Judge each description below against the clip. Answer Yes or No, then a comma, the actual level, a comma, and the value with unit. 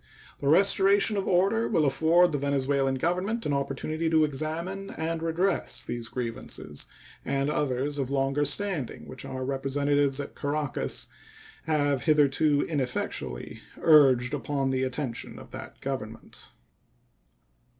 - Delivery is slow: Yes, slow, 125 wpm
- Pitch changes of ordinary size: Yes, average, 3.3 semitones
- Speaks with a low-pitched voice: No, medium, 145 Hz